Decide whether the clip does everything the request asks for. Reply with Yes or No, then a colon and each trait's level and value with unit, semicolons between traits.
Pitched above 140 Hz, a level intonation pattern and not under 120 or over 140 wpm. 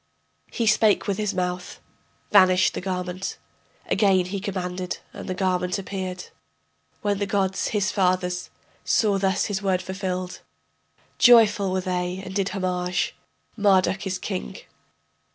Yes: high, 190 Hz; narrow, 1.6 semitones; slow, 135 wpm